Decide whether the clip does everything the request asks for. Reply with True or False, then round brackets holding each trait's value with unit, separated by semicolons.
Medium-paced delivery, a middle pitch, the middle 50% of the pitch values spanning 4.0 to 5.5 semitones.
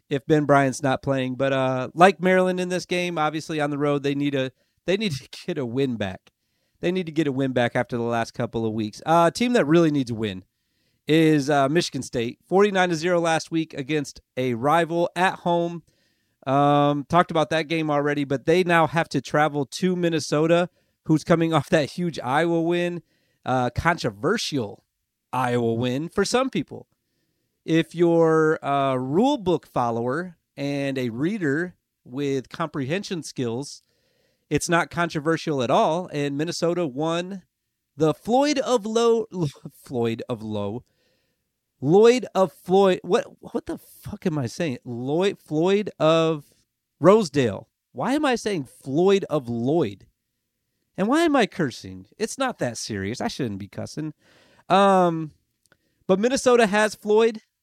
True (160 wpm; 155 Hz; 5.2 semitones)